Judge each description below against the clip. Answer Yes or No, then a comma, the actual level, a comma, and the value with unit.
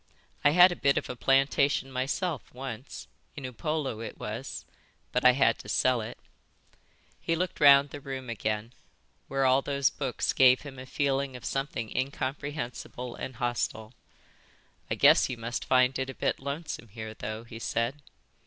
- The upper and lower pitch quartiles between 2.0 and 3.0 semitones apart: Yes, average, 2.7 semitones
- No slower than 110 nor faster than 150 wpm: No, average, 165 wpm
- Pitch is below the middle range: Yes, low, 130 Hz